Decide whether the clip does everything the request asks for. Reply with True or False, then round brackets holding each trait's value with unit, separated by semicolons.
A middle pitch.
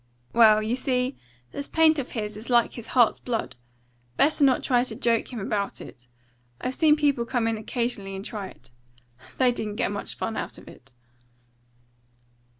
False (235 Hz)